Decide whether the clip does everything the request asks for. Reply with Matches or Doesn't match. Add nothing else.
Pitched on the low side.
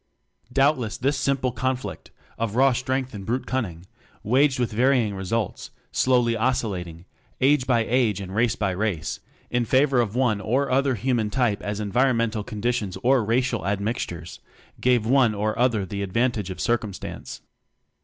Matches